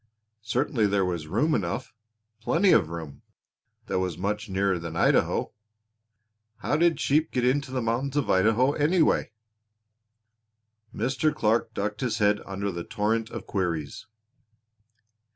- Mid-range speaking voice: No, low, 110 Hz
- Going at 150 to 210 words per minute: No, slow, 135 wpm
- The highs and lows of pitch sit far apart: Yes, wide, 5.7 semitones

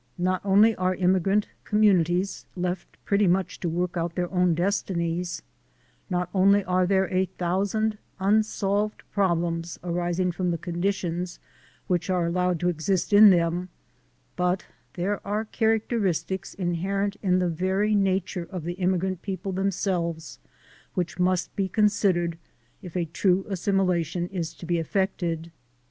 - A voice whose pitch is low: No, medium, 185 Hz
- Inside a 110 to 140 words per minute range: Yes, slow, 135 wpm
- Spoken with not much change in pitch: Yes, narrow, 2.1 semitones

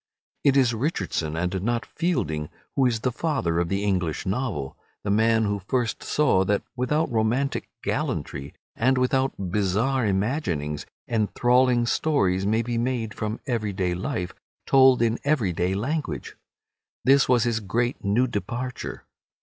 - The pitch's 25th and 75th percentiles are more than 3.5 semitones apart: Yes, average, 5.1 semitones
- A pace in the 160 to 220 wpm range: No, average, 140 wpm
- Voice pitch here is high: No, low, 115 Hz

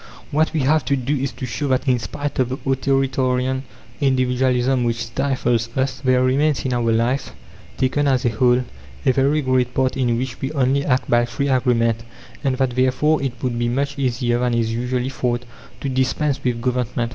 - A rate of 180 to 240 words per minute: Yes, average, 190 wpm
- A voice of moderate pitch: No, low, 130 Hz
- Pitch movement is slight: Yes, narrow, 1.8 semitones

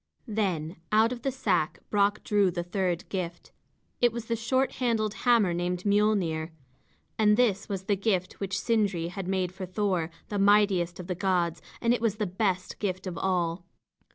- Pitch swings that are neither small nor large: Yes, average, 3.2 semitones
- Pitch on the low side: No, high, 195 Hz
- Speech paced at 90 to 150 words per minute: No, average, 180 wpm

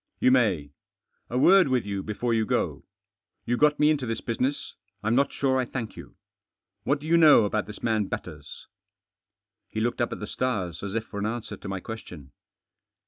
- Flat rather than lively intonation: No, average, 3.9 semitones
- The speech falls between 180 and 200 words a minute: Yes, average, 195 wpm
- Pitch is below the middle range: Yes, low, 115 Hz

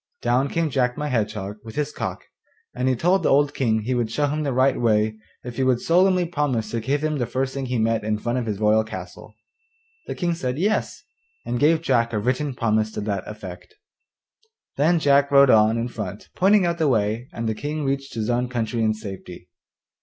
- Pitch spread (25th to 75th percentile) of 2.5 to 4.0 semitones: No, average, 4.8 semitones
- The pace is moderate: No, fast, 215 wpm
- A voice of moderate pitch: No, low, 125 Hz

